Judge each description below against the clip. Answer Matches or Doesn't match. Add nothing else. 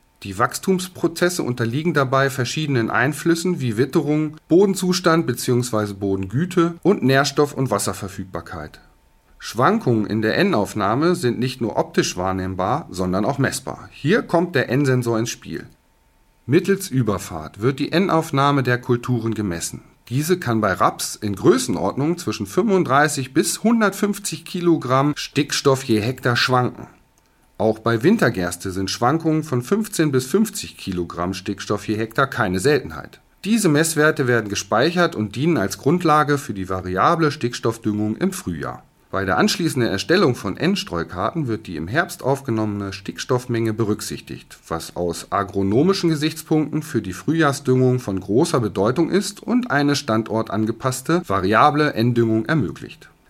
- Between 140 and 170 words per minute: Doesn't match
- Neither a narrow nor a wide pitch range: Doesn't match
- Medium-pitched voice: Doesn't match